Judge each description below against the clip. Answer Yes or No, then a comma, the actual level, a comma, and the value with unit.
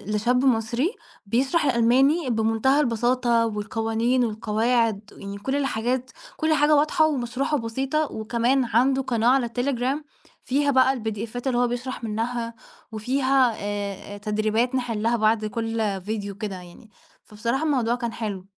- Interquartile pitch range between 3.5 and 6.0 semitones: No, average, 3.1 semitones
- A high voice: Yes, high, 235 Hz